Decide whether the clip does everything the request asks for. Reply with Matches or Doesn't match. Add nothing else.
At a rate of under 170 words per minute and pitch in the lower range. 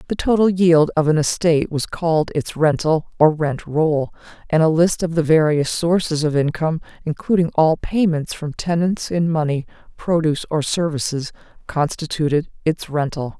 Doesn't match